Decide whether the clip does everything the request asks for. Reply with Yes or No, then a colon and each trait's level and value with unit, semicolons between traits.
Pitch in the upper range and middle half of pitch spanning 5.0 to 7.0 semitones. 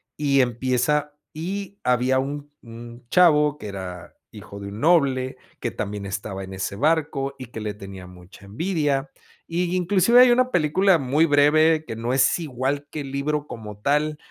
No: medium, 140 Hz; wide, 5.4 semitones